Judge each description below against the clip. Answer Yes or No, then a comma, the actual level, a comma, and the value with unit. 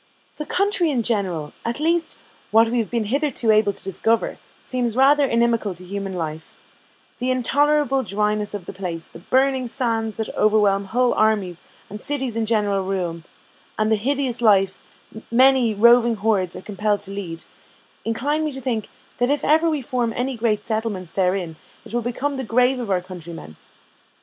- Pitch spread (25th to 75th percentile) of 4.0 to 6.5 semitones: Yes, average, 4.4 semitones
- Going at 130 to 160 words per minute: No, average, 175 wpm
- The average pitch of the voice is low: No, high, 225 Hz